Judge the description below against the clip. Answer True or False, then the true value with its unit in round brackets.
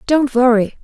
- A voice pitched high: True (250 Hz)